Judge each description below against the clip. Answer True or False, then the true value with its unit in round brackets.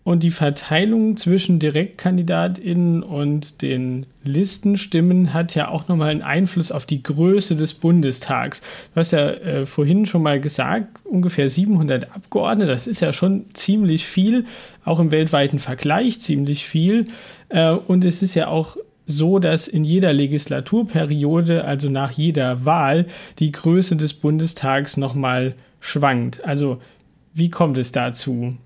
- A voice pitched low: False (165 Hz)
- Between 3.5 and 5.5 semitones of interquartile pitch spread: True (4.1 semitones)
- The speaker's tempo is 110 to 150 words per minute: True (140 wpm)